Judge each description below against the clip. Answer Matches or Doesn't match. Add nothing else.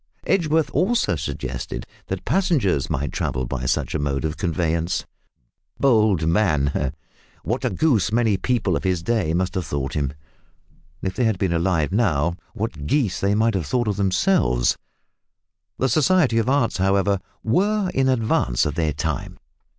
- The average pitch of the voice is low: Matches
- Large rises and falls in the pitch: Matches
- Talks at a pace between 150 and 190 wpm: Matches